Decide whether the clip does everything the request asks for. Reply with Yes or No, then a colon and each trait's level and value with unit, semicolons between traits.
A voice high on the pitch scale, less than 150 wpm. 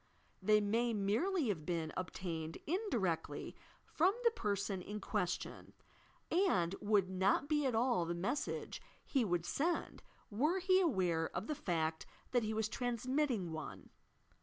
Yes: high, 210 Hz; average, 140 wpm